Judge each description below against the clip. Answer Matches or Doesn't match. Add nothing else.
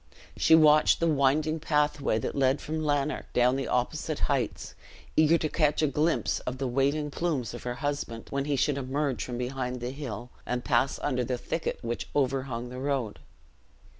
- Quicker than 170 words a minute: Matches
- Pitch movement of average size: Matches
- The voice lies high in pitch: Doesn't match